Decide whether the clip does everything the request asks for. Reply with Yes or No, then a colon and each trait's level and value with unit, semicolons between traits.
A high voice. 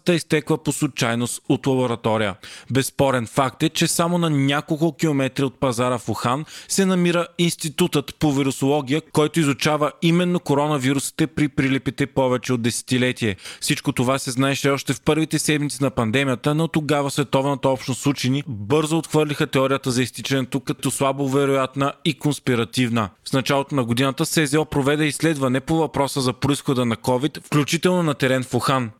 No: medium, 140 Hz